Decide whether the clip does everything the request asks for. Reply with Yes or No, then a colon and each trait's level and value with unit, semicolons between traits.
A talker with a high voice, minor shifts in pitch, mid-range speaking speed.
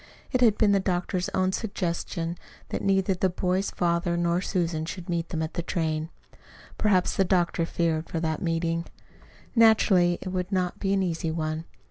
No: medium, 175 Hz; narrow, 2.2 semitones; average, 175 wpm